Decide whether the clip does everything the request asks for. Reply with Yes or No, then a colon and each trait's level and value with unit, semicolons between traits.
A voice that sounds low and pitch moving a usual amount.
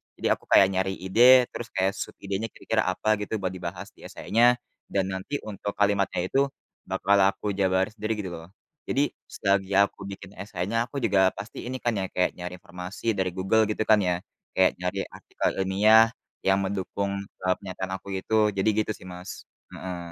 No: very low, 95 Hz; narrow, 1.7 semitones